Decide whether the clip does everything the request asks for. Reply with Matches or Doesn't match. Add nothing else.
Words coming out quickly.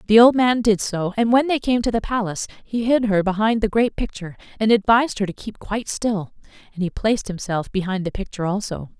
Matches